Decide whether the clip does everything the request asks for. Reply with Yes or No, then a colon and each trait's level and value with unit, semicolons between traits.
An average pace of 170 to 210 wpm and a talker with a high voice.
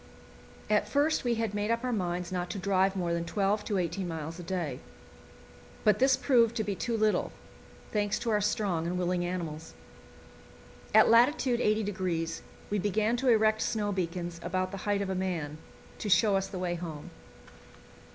Yes: average, 180 wpm; high, 195 Hz